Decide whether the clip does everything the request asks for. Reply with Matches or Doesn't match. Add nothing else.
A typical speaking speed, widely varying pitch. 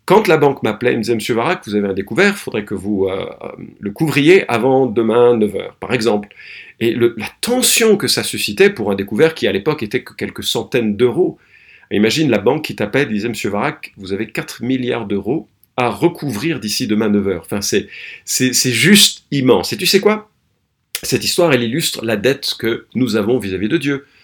Matches